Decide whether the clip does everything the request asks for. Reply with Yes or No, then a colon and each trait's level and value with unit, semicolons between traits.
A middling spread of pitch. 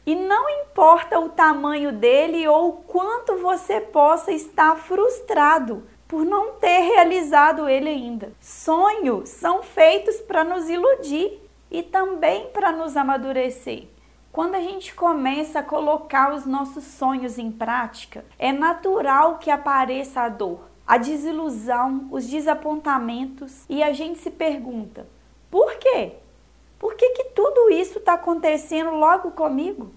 Yes: average, 4.8 semitones